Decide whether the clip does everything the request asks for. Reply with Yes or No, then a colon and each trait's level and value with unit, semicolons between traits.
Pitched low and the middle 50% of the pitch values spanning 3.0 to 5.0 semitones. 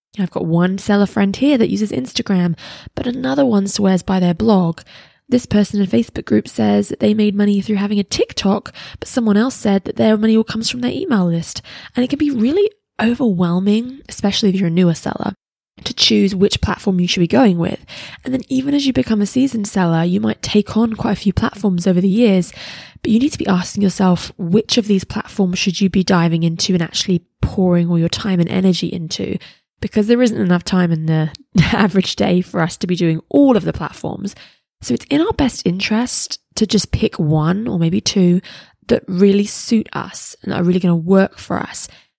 No: high, 200 Hz; average, 3.8 semitones